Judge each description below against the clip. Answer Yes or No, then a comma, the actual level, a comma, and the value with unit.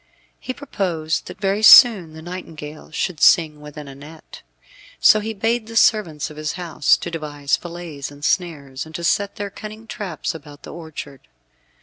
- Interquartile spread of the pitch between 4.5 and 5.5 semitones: Yes, average, 5.1 semitones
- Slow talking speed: No, average, 175 wpm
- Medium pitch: Yes, medium, 165 Hz